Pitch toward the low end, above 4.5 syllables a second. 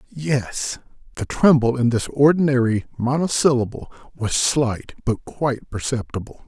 No: low, 125 Hz; 4.4 syllables/s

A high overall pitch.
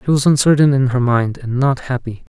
No: low, 130 Hz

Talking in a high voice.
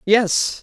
Yes: high, 210 Hz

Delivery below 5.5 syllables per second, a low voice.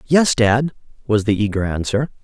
Yes: 5.0 syllables/s; low, 115 Hz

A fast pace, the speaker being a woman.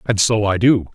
No: fast, 255 wpm; male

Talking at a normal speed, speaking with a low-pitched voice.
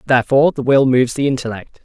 Yes: average, 195 wpm; low, 130 Hz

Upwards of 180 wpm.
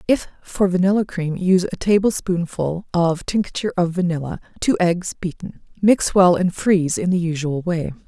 No: average, 170 wpm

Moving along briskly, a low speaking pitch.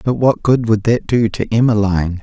Yes: fast, 215 wpm; low, 110 Hz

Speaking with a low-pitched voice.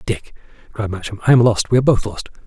Yes: low, 110 Hz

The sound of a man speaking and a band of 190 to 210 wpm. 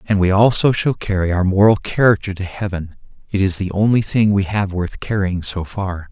Yes: male; fast, 205 wpm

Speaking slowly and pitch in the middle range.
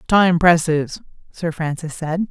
Yes: slow, 130 wpm; medium, 165 Hz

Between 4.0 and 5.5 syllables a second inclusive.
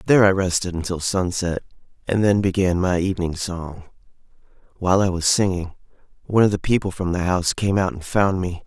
No: 5.9 syllables/s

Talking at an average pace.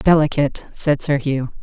Yes: average, 150 wpm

